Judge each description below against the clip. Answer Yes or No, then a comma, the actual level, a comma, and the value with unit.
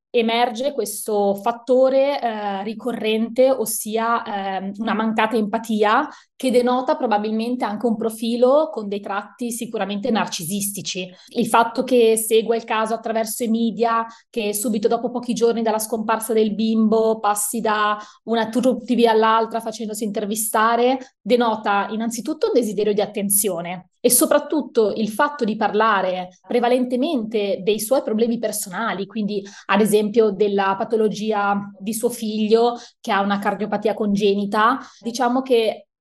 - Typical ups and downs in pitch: No, narrow, 2.1 semitones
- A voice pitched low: No, high, 225 Hz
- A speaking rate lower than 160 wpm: Yes, average, 130 wpm